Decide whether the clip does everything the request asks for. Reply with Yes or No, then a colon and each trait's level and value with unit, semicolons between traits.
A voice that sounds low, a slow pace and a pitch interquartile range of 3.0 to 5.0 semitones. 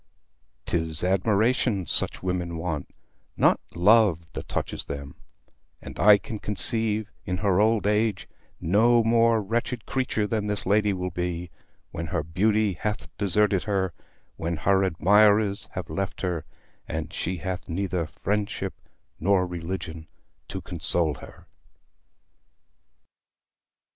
Yes: very low, 95 Hz; slow, 125 wpm; average, 3.5 semitones